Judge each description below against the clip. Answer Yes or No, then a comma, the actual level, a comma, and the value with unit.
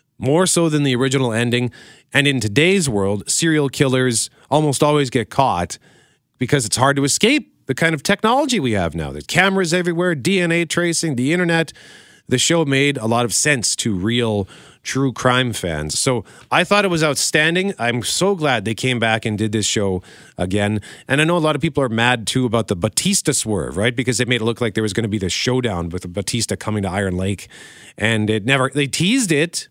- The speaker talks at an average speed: No, fast, 210 wpm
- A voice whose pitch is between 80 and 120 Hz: No, low, 130 Hz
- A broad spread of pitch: Yes, wide, 5.8 semitones